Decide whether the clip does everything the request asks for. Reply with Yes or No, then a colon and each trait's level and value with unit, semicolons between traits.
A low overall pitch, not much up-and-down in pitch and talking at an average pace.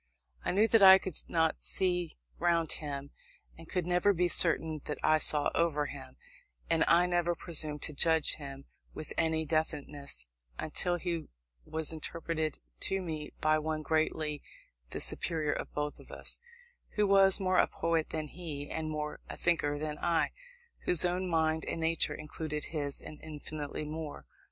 No: medium, 160 Hz; narrow, 2.2 semitones; average, 160 wpm